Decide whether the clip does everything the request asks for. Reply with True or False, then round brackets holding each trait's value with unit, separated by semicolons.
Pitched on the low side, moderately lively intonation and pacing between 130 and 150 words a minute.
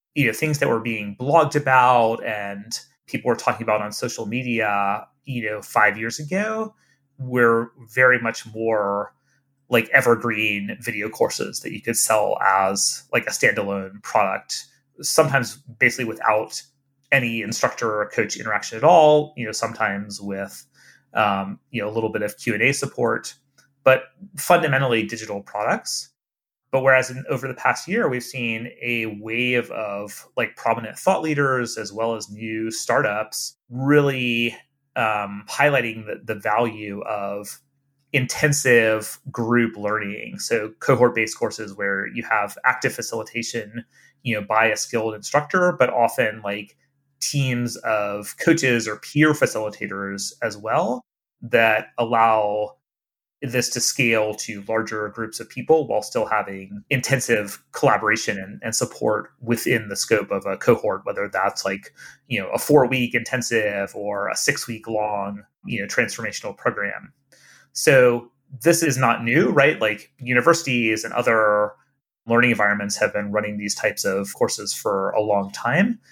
True (115 Hz; 4.0 semitones; 145 wpm)